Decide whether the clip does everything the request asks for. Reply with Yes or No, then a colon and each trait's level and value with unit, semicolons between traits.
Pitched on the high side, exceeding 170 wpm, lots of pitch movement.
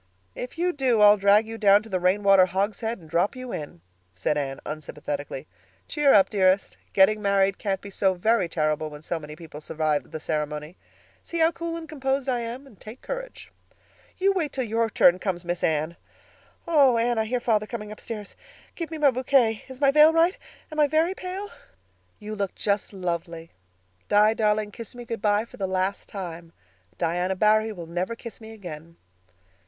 Yes: high, 210 Hz; average, 185 wpm; wide, 5.9 semitones